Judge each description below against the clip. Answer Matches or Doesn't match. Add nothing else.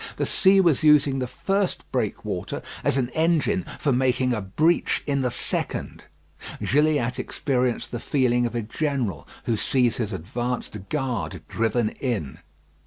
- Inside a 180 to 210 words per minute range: Doesn't match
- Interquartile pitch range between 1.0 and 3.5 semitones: Doesn't match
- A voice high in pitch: Doesn't match